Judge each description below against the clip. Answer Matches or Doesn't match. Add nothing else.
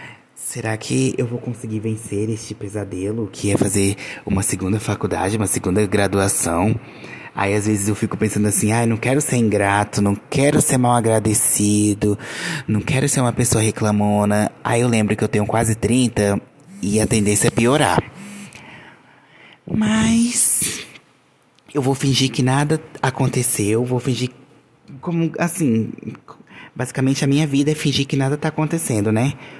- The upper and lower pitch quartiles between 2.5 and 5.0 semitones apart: Matches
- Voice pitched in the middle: Doesn't match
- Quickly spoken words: Doesn't match